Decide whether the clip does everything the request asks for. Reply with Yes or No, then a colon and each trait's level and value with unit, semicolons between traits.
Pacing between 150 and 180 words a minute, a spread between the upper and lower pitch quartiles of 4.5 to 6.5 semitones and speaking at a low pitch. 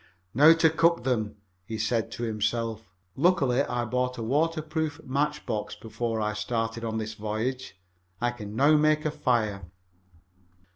Yes: average, 155 wpm; average, 5.1 semitones; low, 120 Hz